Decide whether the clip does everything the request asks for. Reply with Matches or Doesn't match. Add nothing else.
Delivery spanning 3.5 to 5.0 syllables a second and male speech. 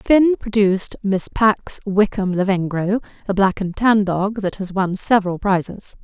Doesn't match